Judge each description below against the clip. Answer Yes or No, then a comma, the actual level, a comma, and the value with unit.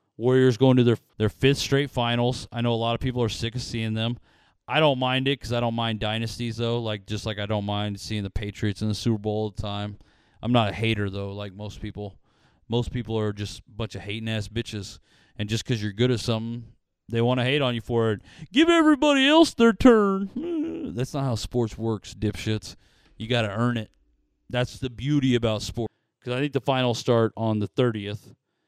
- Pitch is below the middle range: Yes, low, 115 Hz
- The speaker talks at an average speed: No, fast, 225 wpm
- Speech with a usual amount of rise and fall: Yes, average, 3.0 semitones